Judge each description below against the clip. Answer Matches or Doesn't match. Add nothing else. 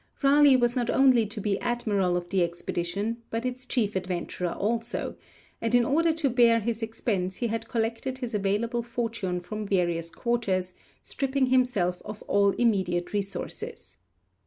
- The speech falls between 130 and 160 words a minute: Matches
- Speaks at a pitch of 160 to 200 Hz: Doesn't match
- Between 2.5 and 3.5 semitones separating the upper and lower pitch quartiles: Doesn't match